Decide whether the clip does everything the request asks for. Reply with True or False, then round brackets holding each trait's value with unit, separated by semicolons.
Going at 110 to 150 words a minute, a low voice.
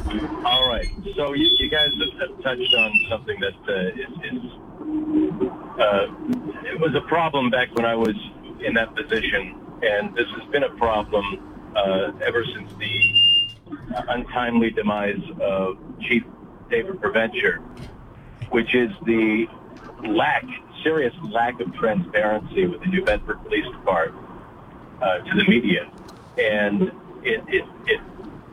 True (135 wpm; 125 Hz)